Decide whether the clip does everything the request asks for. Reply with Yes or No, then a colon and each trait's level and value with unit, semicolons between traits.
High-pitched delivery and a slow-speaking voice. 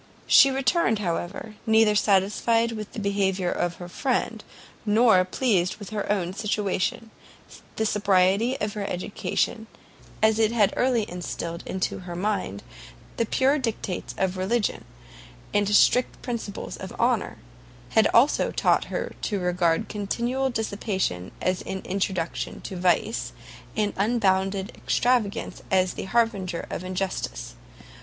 Yes: high, 205 Hz; slow, 130 wpm